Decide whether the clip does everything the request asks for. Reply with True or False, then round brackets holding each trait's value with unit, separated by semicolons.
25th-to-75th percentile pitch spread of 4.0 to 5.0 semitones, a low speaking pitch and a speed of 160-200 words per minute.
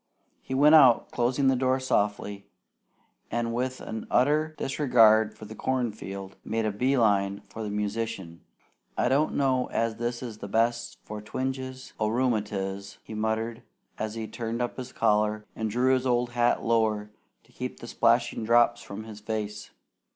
False (3.1 semitones; 115 Hz; 170 wpm)